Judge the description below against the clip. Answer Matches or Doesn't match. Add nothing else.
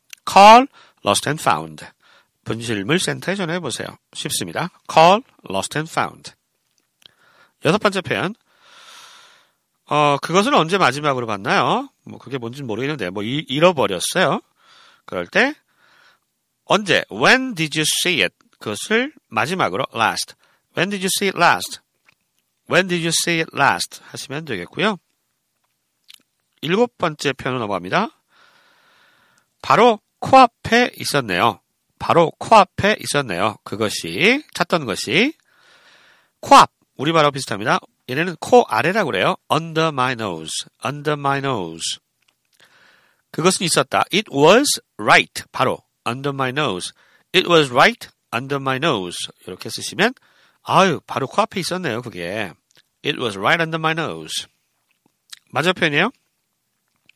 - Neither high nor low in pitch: Matches